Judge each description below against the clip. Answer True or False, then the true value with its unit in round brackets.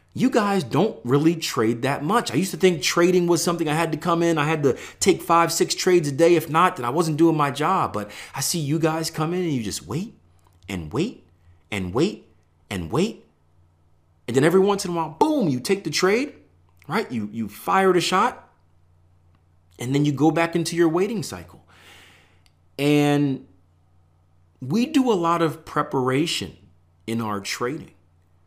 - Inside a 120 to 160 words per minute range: False (190 wpm)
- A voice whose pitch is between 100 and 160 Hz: True (140 Hz)